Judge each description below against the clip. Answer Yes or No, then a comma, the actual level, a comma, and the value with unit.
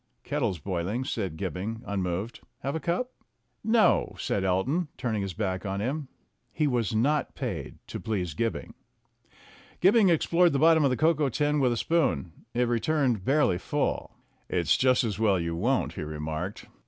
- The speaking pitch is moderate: No, low, 115 Hz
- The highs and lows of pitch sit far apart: Yes, wide, 7.8 semitones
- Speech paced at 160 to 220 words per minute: Yes, average, 165 wpm